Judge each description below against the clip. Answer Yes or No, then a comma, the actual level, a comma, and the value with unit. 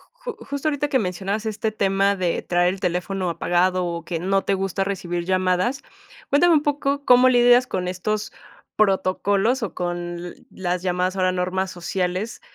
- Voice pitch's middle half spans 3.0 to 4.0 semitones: Yes, average, 3.5 semitones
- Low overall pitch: No, high, 190 Hz